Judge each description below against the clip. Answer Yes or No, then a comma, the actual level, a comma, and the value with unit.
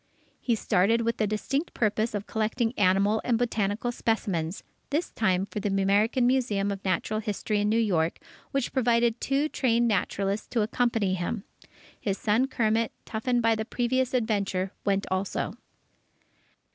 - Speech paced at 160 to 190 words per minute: No, average, 150 wpm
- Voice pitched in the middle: No, high, 220 Hz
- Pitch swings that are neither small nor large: Yes, average, 3.1 semitones